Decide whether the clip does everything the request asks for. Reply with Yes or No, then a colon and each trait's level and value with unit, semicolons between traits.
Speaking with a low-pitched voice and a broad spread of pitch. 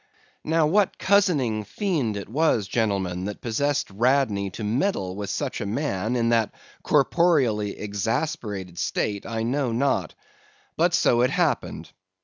Yes: low, 115 Hz; wide, 5.9 semitones